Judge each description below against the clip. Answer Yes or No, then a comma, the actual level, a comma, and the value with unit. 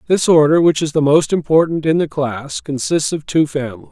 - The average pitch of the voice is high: No, medium, 150 Hz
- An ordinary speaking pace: No, fast, 215 wpm